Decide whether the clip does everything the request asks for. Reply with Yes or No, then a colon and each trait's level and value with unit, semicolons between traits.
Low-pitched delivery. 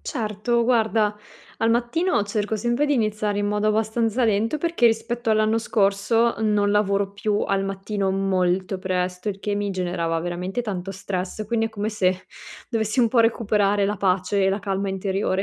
No: high, 205 Hz